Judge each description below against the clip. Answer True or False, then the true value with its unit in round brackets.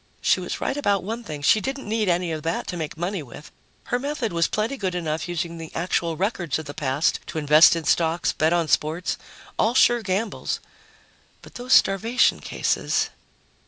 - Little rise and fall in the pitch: False (5.3 semitones)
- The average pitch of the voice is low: False (175 Hz)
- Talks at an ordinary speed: True (190 wpm)